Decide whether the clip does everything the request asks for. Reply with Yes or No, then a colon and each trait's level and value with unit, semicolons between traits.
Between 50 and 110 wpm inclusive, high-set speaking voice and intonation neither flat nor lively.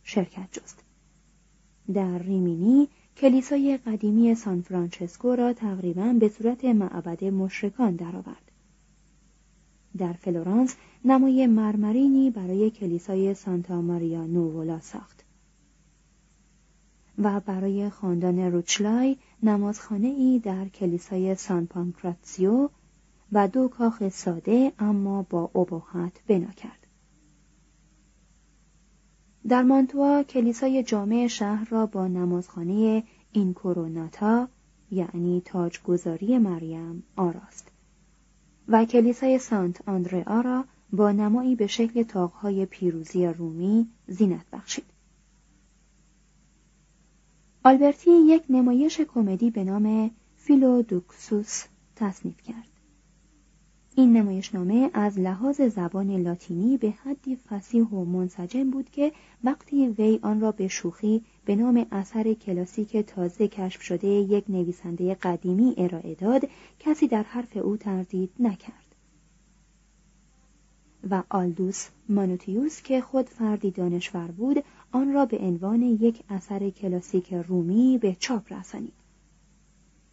Yes: slow, 105 wpm; high, 195 Hz; average, 4.4 semitones